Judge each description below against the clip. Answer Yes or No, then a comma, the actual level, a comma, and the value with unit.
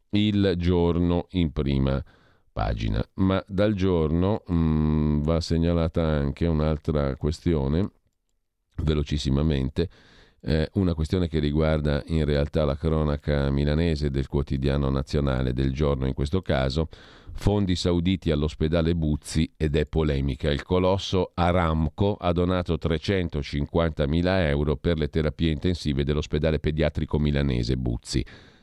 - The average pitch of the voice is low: Yes, very low, 80 Hz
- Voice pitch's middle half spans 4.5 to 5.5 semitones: No, average, 3.0 semitones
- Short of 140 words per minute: Yes, slow, 115 wpm